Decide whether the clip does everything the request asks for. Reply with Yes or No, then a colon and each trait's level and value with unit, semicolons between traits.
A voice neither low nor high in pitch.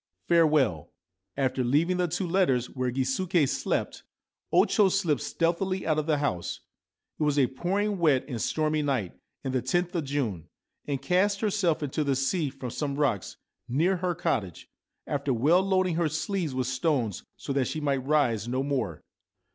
Yes: medium, 145 Hz